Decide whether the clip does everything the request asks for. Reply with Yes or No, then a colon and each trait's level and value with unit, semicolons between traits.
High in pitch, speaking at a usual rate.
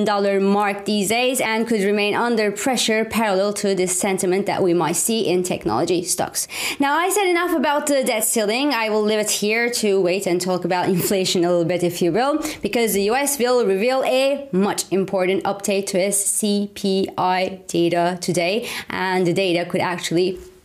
Yes: high, 200 Hz; average, 185 wpm